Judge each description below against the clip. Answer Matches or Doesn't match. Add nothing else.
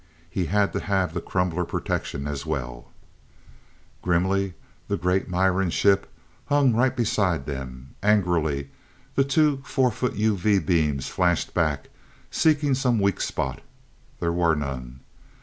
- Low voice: Matches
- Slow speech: Matches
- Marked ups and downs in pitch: Matches